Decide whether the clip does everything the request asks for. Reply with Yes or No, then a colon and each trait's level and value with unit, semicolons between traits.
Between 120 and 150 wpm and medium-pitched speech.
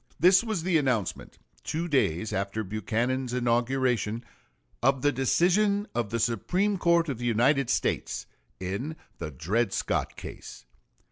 No: slow, 135 wpm; low, 125 Hz